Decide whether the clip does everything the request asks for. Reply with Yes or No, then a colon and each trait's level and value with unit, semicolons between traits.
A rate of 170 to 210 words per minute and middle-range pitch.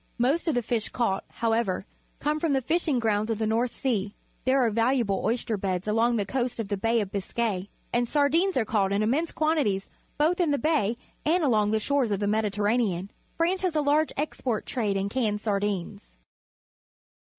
No: average, 190 wpm; high, 230 Hz